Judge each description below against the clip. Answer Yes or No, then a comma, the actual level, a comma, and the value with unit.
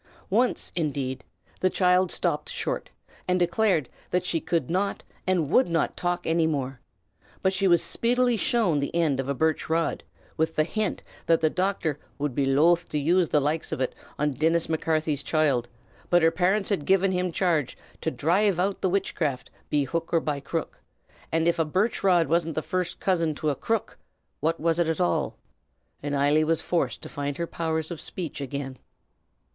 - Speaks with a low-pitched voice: No, medium, 165 Hz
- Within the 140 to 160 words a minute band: No, average, 185 wpm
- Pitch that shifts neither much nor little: Yes, average, 3.4 semitones